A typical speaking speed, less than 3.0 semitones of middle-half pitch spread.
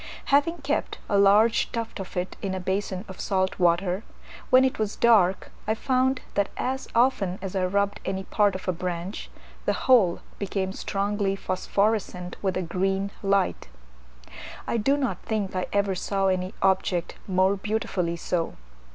Yes: average, 160 wpm; narrow, 2.6 semitones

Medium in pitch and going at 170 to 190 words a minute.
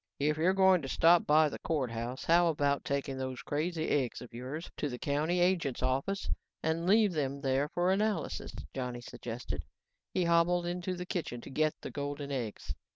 Yes: medium, 150 Hz; average, 180 wpm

